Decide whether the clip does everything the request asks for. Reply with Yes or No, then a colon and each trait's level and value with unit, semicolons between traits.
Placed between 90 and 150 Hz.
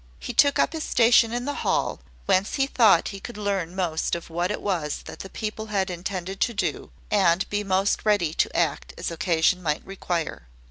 No: high, 195 Hz